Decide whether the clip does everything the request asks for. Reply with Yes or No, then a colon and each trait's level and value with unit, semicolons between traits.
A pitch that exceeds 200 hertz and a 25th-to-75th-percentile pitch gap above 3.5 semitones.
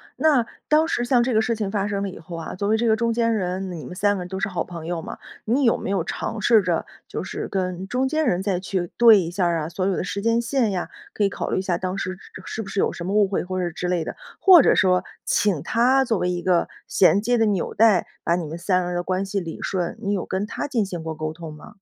No: high, 195 Hz; average, 3.9 semitones